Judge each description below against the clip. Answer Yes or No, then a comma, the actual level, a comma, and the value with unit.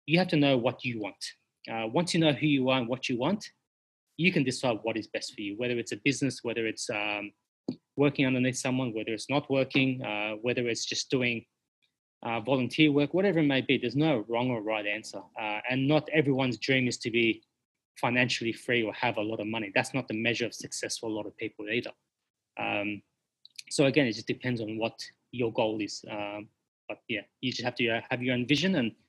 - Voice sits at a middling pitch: No, low, 125 Hz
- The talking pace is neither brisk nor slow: No, fast, 230 wpm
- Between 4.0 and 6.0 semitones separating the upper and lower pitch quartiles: No, average, 3.3 semitones